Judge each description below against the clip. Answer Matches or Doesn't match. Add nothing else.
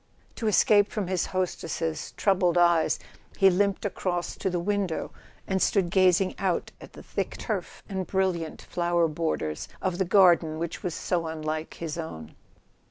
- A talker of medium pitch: Matches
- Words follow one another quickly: Doesn't match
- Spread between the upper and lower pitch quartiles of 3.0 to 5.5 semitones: Doesn't match